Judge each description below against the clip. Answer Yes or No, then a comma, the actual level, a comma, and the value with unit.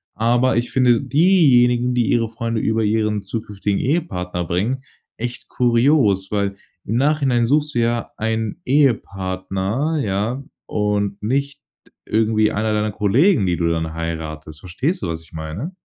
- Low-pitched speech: Yes, low, 110 Hz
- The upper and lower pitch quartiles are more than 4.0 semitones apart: Yes, average, 4.5 semitones